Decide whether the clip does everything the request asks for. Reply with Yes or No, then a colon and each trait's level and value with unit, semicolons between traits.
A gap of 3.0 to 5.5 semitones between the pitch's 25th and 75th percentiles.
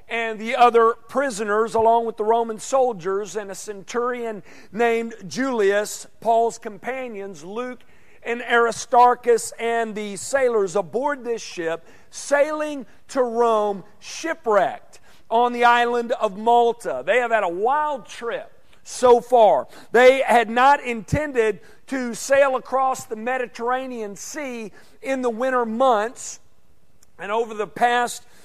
No: narrow, 2.5 semitones